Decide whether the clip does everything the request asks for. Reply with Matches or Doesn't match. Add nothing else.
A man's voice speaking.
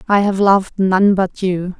Doesn't match